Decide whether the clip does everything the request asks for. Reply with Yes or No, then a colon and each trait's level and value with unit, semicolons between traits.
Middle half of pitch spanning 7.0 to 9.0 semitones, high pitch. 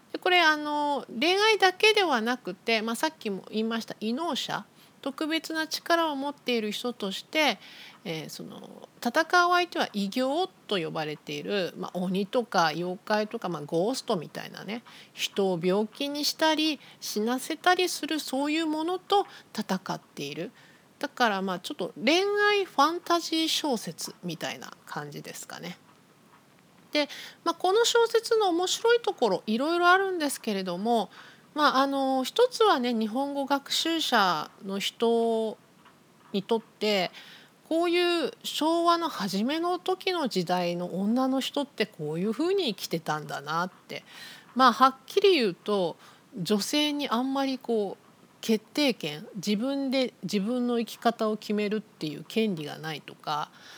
Yes: wide, 7.8 semitones; high, 245 Hz